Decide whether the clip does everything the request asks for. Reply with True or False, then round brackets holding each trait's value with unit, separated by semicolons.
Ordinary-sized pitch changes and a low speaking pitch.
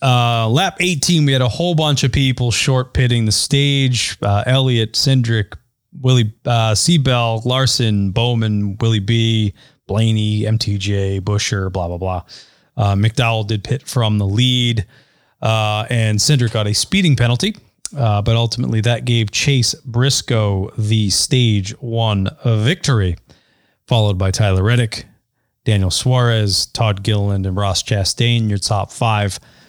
True (3.5 semitones; 115 Hz)